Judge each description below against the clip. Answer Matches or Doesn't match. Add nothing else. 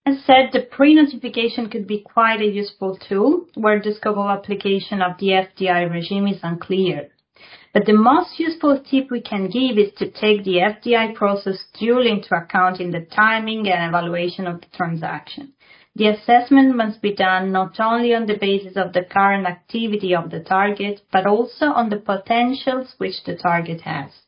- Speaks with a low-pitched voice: Doesn't match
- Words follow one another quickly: Doesn't match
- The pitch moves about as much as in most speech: Matches